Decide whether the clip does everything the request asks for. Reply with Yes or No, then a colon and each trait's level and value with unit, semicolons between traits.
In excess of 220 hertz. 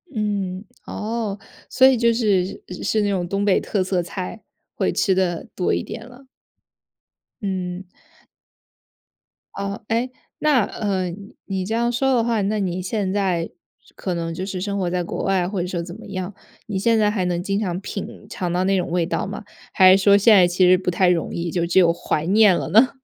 No: high, 195 Hz